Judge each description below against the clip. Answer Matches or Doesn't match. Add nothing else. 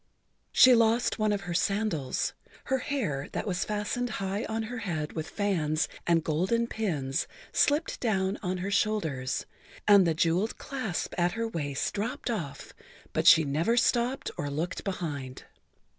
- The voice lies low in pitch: Doesn't match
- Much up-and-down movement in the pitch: Matches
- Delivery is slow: Doesn't match